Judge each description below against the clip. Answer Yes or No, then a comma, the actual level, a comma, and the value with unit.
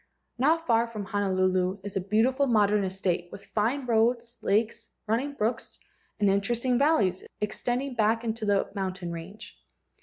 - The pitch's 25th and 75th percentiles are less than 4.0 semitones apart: Yes, average, 3.5 semitones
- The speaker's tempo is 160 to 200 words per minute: No, average, 145 wpm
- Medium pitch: No, high, 215 Hz